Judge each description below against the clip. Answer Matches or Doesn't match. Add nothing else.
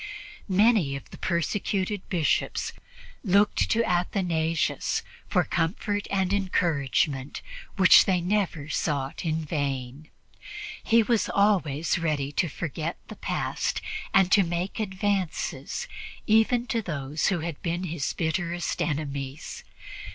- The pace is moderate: Doesn't match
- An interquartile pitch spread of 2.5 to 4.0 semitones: Doesn't match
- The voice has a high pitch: Doesn't match